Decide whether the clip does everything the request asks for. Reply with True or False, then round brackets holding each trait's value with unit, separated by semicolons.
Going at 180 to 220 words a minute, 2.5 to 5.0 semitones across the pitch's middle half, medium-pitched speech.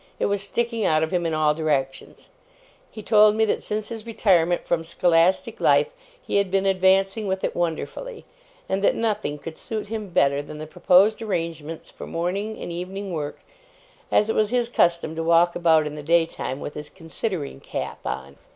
True (190 wpm; 4.7 semitones; 175 Hz)